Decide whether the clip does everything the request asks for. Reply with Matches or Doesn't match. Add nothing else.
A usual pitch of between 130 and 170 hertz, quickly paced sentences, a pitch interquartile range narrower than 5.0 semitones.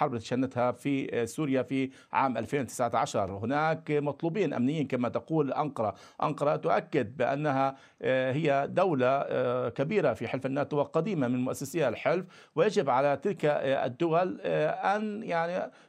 Doesn't match